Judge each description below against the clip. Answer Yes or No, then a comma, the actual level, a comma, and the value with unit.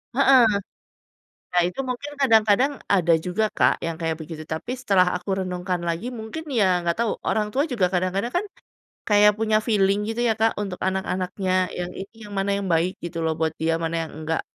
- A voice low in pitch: No, high, 195 Hz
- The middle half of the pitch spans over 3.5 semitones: Yes, average, 4.0 semitones